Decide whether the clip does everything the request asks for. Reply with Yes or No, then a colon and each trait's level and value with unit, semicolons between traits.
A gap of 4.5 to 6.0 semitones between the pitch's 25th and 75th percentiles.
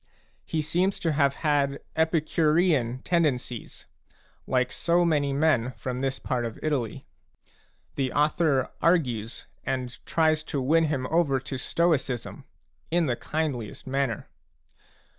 No: average, 3.8 semitones